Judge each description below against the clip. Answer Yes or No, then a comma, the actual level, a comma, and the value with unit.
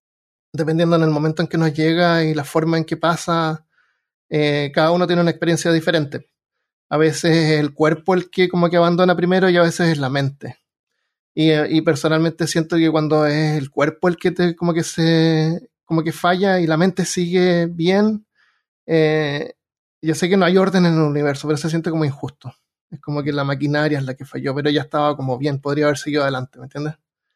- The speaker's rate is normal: No, fast, 210 wpm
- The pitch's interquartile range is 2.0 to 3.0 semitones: Yes, narrow, 2.4 semitones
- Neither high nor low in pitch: Yes, medium, 160 Hz